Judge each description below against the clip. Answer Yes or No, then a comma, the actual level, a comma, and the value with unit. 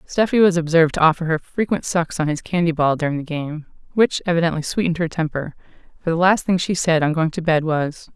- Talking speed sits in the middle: No, fast, 230 wpm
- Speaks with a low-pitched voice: No, medium, 165 Hz